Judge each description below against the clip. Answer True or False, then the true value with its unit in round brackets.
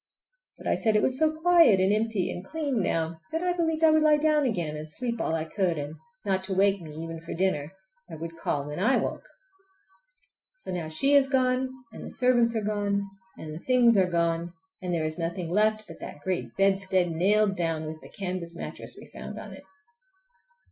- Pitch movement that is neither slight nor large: False (6.6 semitones)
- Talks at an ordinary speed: False (210 wpm)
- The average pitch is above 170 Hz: True (190 Hz)